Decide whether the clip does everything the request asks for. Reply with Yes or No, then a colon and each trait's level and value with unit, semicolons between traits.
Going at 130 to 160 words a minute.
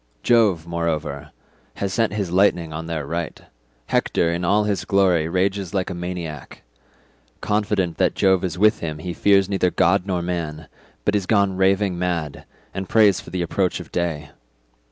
No: average, 170 wpm